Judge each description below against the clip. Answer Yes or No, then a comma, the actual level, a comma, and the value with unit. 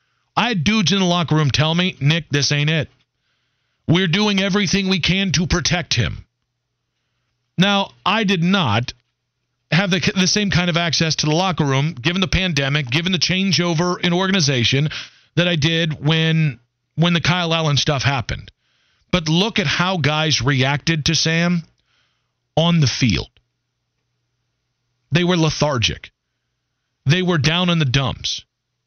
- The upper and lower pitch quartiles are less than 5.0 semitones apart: No, wide, 5.6 semitones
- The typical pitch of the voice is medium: Yes, medium, 155 Hz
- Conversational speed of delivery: Yes, average, 155 wpm